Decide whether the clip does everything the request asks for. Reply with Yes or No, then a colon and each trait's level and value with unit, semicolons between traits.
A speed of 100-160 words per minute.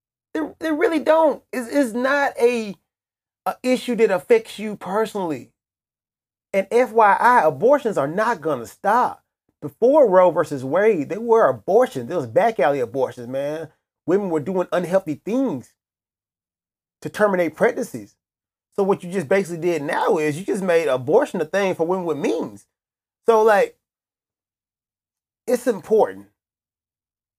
Yes: average, 140 wpm